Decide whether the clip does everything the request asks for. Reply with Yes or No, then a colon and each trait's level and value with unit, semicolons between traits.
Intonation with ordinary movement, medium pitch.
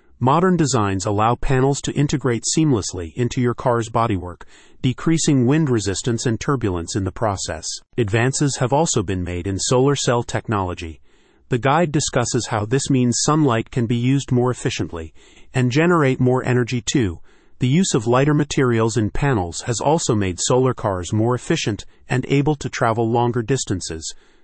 No: average, 4.1 semitones; low, 125 Hz